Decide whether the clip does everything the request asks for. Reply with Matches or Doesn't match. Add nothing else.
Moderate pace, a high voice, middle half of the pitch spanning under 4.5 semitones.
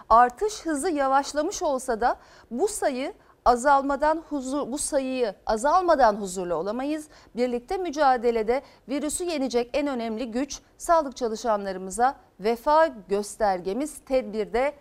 Matches